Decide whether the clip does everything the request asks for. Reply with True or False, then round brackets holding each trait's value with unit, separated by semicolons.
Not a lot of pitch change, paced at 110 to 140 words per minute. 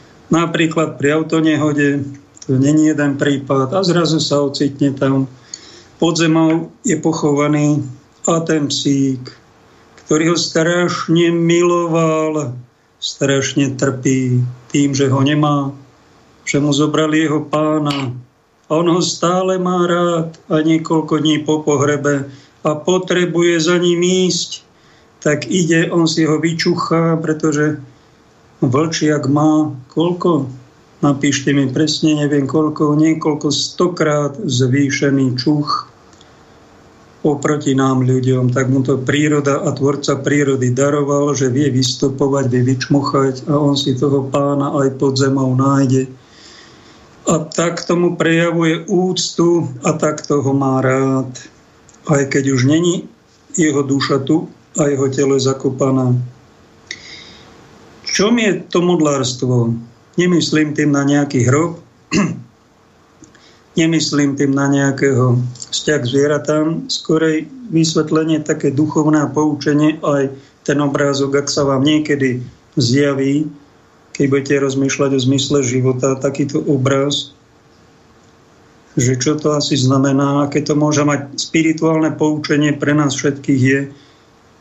True (2.3 semitones; 120 wpm)